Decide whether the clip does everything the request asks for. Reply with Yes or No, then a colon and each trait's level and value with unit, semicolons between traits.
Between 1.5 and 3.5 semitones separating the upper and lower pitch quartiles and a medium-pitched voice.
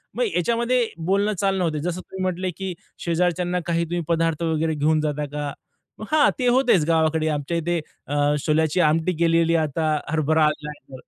Yes: average, 2.9 semitones; medium, 165 Hz